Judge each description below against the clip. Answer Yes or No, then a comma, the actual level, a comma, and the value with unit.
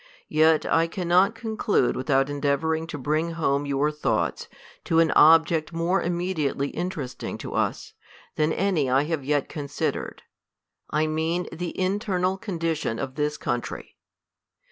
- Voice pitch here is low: No, medium, 160 Hz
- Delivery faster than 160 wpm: No, average, 145 wpm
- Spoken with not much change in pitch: No, average, 3.3 semitones